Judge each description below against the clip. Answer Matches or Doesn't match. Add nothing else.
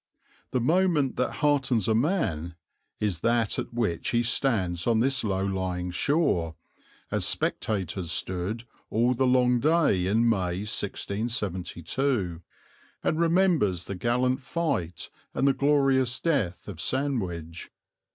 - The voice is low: Matches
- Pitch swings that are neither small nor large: Doesn't match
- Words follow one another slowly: Matches